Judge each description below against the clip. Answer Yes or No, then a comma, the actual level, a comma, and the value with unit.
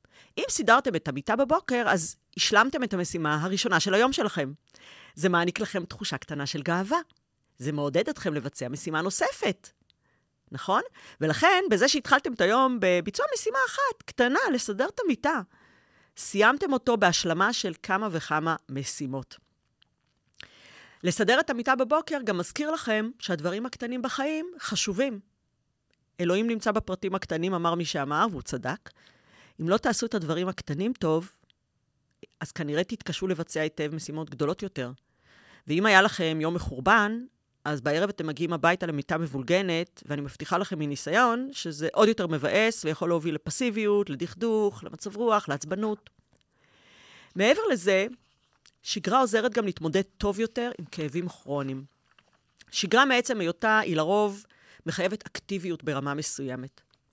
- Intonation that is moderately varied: No, wide, 6.4 semitones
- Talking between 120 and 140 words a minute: Yes, average, 135 wpm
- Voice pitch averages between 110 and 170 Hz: No, medium, 185 Hz